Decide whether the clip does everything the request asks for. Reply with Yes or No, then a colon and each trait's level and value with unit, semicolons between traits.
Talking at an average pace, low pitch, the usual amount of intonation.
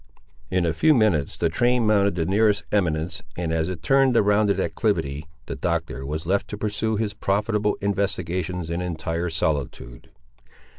Yes: average, 160 wpm; very low, 95 Hz; average, 4.3 semitones